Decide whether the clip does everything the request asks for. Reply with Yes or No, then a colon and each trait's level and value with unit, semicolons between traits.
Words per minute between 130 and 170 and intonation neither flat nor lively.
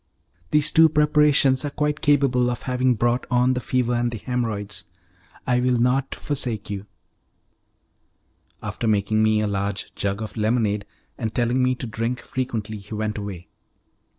Yes: average, 160 wpm; average, 3.3 semitones